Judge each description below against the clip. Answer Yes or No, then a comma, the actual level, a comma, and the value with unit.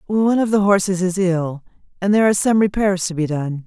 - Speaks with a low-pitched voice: No, high, 190 Hz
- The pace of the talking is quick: Yes, fast, 230 wpm